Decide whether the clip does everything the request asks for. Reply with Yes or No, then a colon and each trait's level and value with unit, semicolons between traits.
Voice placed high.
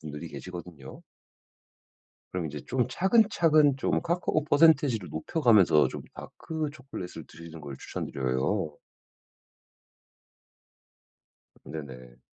No: very low, 90 Hz